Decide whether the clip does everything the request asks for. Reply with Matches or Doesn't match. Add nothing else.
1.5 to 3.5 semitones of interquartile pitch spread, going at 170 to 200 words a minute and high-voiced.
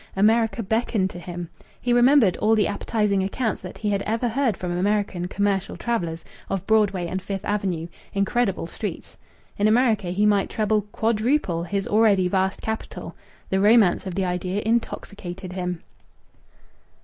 Doesn't match